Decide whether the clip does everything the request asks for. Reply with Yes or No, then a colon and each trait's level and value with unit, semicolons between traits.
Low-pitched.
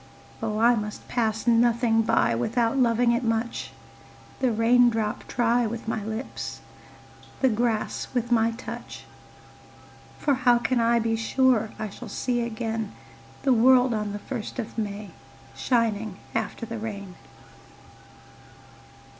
No: high, 230 Hz